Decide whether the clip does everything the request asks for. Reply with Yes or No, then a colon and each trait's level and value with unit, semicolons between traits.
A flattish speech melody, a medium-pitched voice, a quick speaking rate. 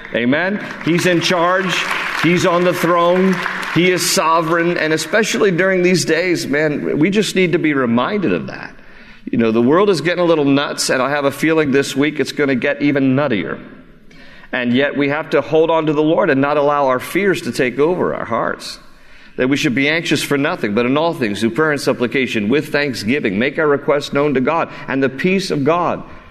No: average, 3.7 semitones; medium, 155 Hz; fast, 215 wpm